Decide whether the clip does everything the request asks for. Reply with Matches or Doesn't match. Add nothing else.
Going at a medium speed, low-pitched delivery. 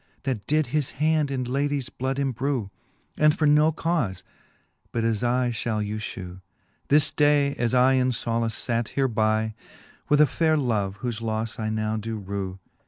Matches